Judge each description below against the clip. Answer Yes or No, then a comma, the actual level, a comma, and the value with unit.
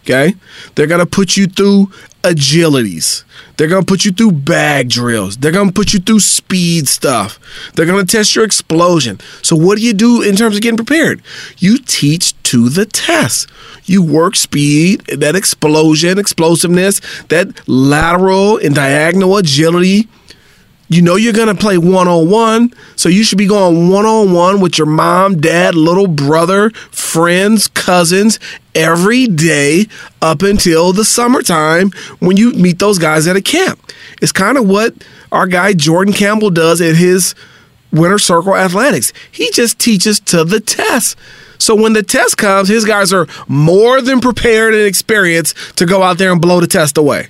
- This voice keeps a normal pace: Yes, average, 170 wpm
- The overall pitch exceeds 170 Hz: Yes, medium, 185 Hz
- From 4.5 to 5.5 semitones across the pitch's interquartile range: No, average, 4.1 semitones